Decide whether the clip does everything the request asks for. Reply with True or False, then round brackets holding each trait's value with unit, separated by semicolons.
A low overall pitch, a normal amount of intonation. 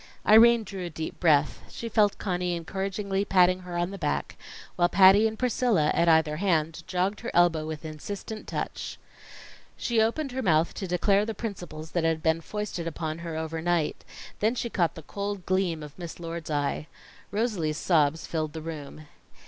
False (175 Hz; 4.0 semitones)